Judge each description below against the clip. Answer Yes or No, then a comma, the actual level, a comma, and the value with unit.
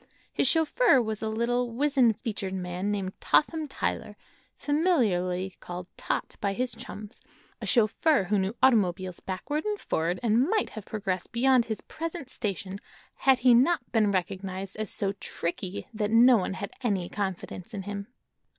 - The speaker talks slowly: No, average, 160 wpm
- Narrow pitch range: No, average, 4.9 semitones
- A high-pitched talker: Yes, high, 215 Hz